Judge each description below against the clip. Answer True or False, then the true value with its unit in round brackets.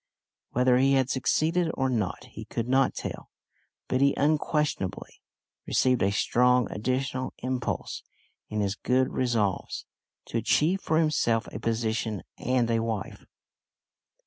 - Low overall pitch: True (125 Hz)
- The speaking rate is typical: False (130 wpm)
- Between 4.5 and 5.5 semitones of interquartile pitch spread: False (2.9 semitones)